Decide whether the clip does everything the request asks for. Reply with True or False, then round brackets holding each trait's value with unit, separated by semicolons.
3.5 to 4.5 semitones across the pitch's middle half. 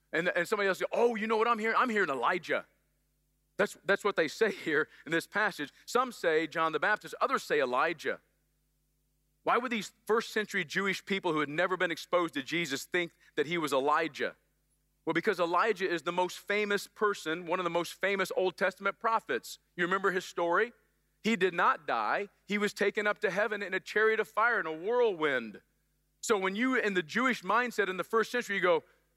True (3.8 semitones)